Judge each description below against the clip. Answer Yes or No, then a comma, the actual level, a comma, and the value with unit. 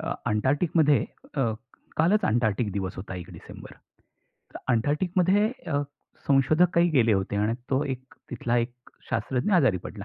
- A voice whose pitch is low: Yes, low, 130 Hz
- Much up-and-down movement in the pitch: Yes, wide, 6.2 semitones